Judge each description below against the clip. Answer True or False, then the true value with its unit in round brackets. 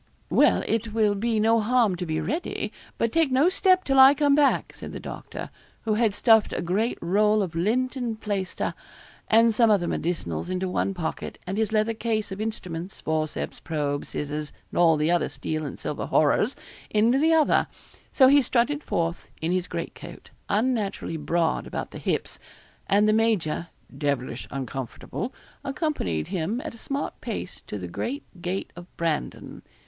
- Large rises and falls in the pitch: True (6.1 semitones)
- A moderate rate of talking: True (175 wpm)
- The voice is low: False (210 Hz)